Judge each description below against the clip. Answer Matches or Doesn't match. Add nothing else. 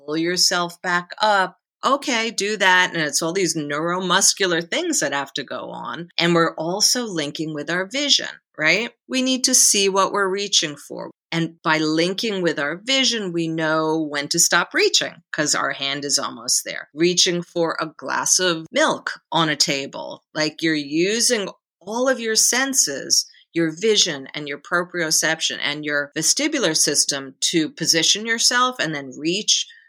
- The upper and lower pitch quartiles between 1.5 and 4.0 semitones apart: Doesn't match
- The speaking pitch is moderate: Matches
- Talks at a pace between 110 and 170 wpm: Matches